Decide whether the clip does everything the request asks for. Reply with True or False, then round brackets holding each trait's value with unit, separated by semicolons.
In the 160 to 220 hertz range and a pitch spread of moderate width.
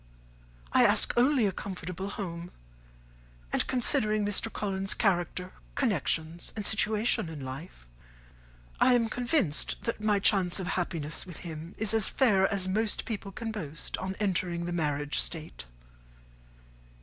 True (190 Hz; 4.1 semitones)